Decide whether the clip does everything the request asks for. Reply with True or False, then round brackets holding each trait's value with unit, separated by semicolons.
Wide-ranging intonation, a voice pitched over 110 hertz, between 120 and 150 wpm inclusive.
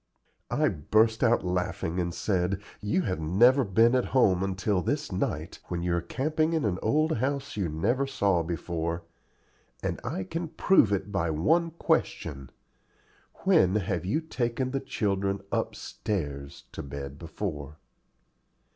False (6.7 semitones; 100 Hz; 145 wpm)